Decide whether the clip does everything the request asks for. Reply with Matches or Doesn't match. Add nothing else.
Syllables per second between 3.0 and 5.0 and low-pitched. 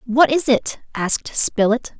Doesn't match